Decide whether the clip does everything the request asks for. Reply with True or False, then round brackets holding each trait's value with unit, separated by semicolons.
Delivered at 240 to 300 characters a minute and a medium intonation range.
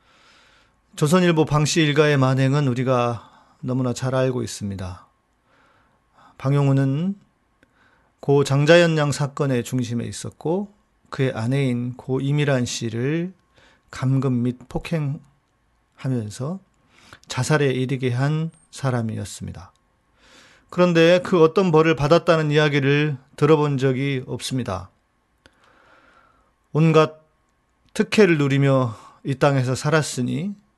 False (230 characters per minute; 3.7 semitones)